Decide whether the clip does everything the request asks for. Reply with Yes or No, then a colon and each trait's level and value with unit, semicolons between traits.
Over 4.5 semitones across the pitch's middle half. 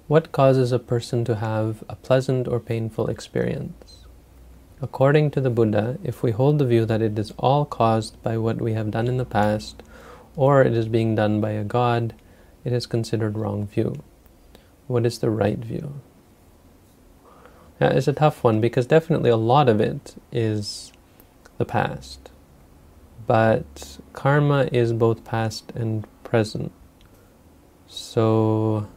No: average, 3.2 semitones